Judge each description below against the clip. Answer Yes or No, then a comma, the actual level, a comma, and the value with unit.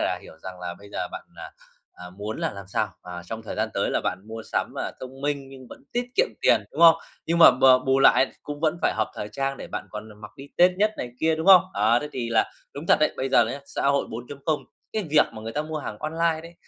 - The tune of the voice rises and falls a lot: Yes, wide, 6.2 semitones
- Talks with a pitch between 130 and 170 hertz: Yes, low, 135 Hz